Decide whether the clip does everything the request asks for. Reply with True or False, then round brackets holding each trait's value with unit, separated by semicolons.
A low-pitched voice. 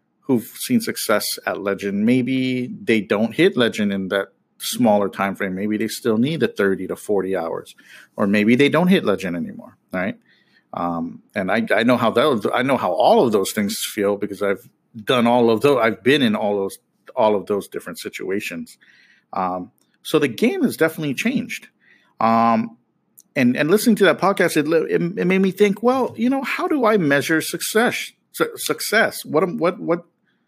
True (130 Hz)